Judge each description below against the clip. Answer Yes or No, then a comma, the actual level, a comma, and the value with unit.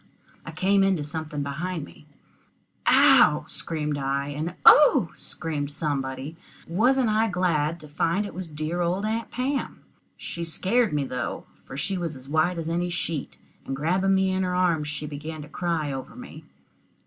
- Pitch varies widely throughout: No, average, 3.9 semitones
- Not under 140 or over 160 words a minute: No, average, 170 wpm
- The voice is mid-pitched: Yes, medium, 165 Hz